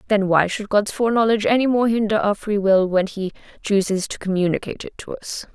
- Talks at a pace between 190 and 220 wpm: Yes, fast, 205 wpm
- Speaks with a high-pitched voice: Yes, high, 205 Hz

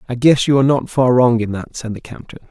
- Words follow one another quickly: Yes, fast, 285 wpm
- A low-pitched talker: Yes, low, 125 Hz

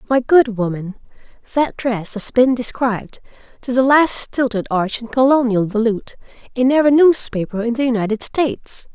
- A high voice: Yes, high, 240 Hz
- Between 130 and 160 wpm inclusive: Yes, average, 155 wpm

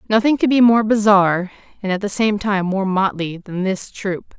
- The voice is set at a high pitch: Yes, high, 200 Hz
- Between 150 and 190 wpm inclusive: No, fast, 205 wpm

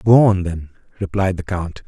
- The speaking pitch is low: Yes, very low, 95 Hz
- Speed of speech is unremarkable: Yes, average, 190 wpm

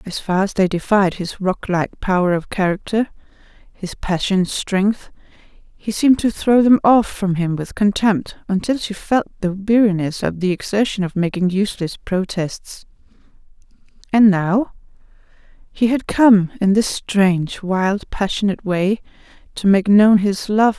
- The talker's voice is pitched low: No, high, 195 Hz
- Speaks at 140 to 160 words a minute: Yes, average, 150 wpm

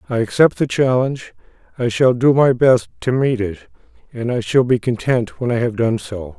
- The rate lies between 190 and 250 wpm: Yes, fast, 205 wpm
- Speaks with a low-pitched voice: Yes, low, 120 Hz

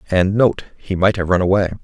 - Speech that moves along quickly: Yes, fast, 230 wpm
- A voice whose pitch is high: No, very low, 95 Hz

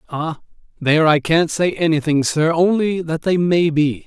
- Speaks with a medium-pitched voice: Yes, medium, 160 Hz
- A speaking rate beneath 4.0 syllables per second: No, 4.7 syllables/s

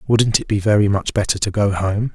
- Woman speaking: No, male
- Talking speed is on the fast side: Yes, fast, 250 wpm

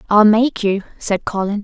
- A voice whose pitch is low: No, high, 210 Hz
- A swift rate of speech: No, average, 185 wpm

